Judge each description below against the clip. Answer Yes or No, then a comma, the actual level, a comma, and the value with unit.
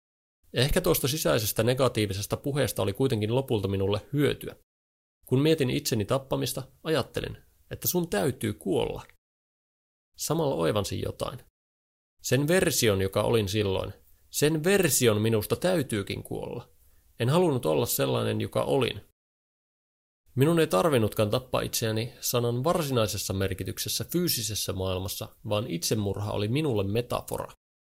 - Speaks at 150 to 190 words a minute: No, average, 115 wpm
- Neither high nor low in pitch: No, low, 110 Hz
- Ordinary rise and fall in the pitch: No, wide, 6.0 semitones